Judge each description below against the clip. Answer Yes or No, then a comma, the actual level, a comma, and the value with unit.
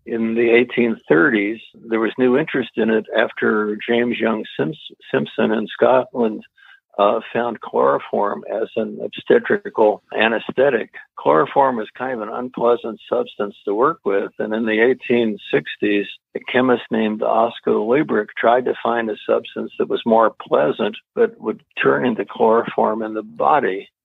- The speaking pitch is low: Yes, low, 115 Hz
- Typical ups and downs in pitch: No, narrow, 2.3 semitones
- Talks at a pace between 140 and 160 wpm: Yes, average, 145 wpm